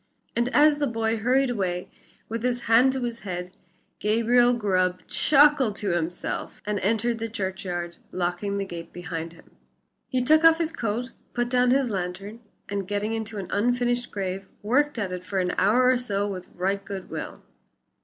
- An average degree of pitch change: Yes, average, 4.5 semitones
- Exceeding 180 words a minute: No, average, 175 wpm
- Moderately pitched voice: No, high, 215 Hz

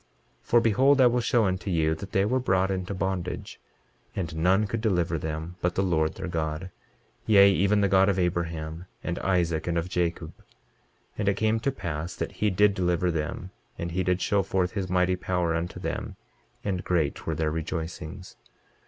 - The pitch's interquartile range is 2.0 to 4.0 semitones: Yes, average, 2.8 semitones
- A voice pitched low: Yes, very low, 90 Hz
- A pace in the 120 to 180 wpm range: No, average, 195 wpm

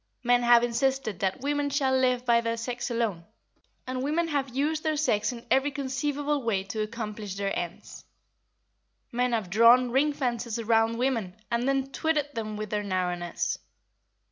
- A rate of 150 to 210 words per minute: Yes, average, 165 wpm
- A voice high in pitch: Yes, high, 240 Hz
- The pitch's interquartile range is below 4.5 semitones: Yes, average, 3.8 semitones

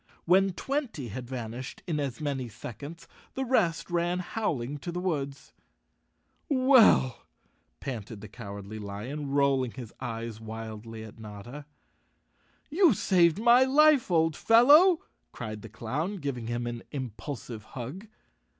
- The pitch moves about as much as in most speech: No, wide, 7.9 semitones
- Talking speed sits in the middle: No, slow, 130 wpm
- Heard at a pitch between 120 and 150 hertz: Yes, medium, 140 Hz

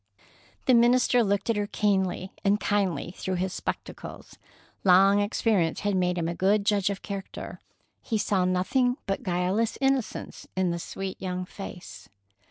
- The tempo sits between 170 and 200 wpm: No, average, 155 wpm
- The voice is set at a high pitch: Yes, high, 195 Hz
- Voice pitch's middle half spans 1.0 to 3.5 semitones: Yes, narrow, 2.5 semitones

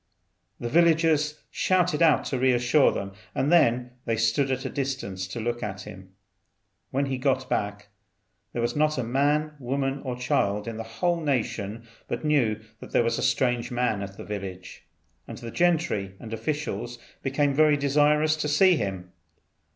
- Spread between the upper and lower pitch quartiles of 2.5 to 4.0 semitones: No, average, 4.9 semitones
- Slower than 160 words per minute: No, average, 175 wpm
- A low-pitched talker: Yes, low, 125 Hz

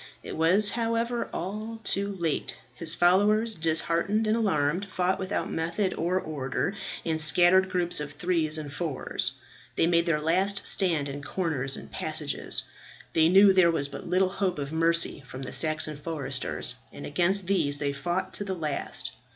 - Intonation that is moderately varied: Yes, average, 3.9 semitones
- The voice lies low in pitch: No, medium, 170 Hz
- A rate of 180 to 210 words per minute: No, average, 165 wpm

